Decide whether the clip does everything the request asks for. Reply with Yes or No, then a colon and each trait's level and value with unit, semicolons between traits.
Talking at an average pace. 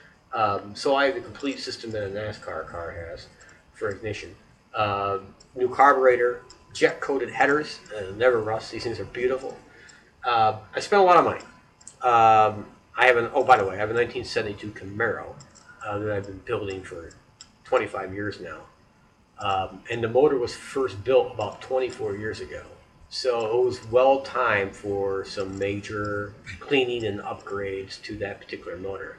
Yes: average, 170 wpm